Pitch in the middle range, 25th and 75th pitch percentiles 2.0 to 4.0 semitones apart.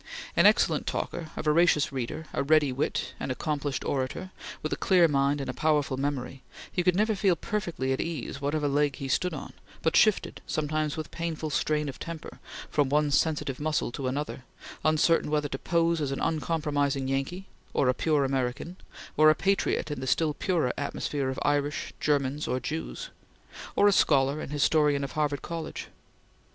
Yes: medium, 150 Hz; average, 2.7 semitones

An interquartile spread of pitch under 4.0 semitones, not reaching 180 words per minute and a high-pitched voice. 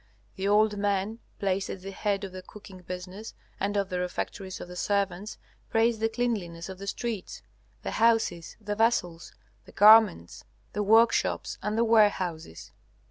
Yes: average, 2.9 semitones; average, 160 wpm; high, 200 Hz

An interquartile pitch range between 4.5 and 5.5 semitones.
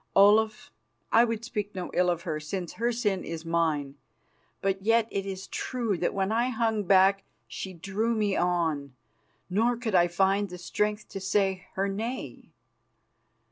No: average, 3.6 semitones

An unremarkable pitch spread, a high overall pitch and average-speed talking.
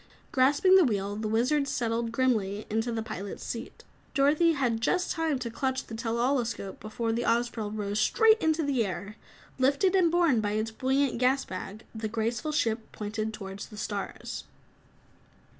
Yes: average, 4.3 semitones; high, 235 Hz; average, 170 wpm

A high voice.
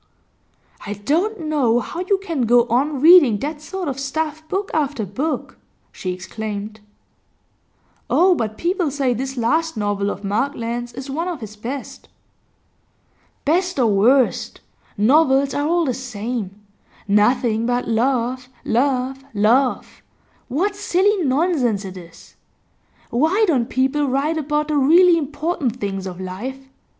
Yes: very high, 265 Hz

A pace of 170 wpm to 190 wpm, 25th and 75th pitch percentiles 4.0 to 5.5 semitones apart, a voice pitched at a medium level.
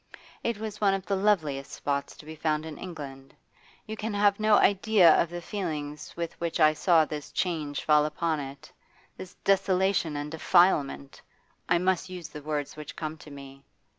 Yes: average, 180 wpm; average, 4.3 semitones; medium, 160 Hz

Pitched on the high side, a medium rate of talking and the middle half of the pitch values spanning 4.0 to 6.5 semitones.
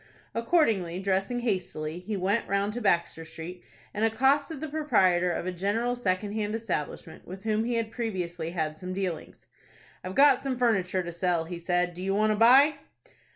Yes: high, 195 Hz; average, 180 wpm; average, 4.5 semitones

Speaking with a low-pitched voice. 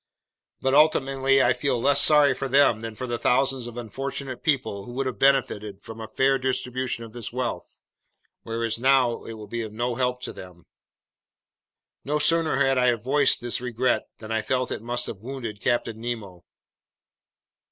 Yes: low, 125 Hz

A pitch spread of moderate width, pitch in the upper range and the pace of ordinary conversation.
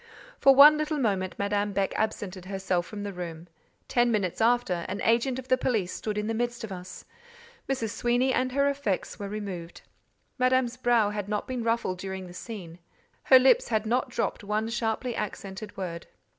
Yes: average, 4.2 semitones; high, 215 Hz; average, 180 wpm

